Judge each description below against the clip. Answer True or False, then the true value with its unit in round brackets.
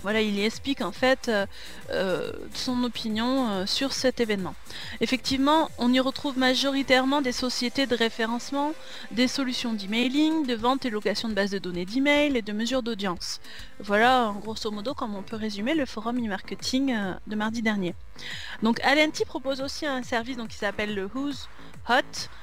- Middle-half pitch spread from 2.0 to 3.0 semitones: False (3.7 semitones)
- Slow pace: False (175 wpm)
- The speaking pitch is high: True (245 Hz)